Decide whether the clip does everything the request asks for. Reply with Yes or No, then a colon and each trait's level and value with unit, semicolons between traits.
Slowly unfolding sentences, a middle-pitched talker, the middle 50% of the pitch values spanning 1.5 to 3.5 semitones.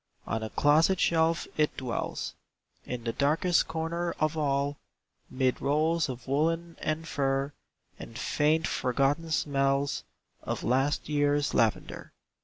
Yes: slow, 125 wpm; medium, 145 Hz; average, 2.9 semitones